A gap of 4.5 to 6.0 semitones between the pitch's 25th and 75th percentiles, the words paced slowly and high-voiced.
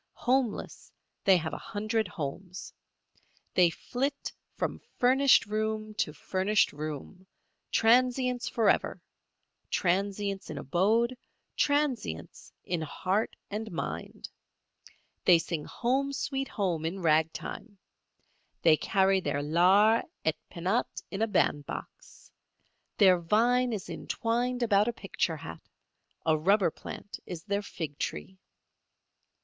Yes: average, 5.1 semitones; slow, 110 wpm; high, 200 Hz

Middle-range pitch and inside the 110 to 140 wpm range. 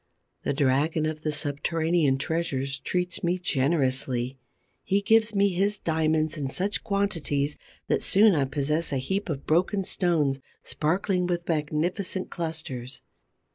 Yes: medium, 160 Hz; slow, 135 wpm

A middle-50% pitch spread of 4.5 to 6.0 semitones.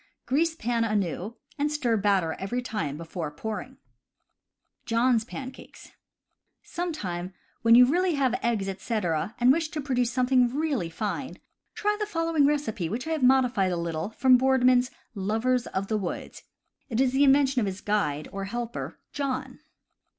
Yes: average, 5.2 semitones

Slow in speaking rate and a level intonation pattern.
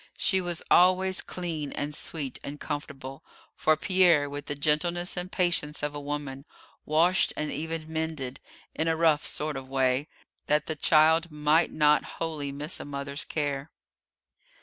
No: average, 160 wpm; narrow, 2.2 semitones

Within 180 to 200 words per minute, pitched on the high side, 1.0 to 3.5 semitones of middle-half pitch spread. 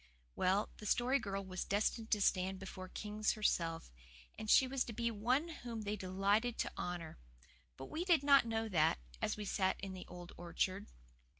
No: average, 185 wpm; high, 205 Hz; average, 3.9 semitones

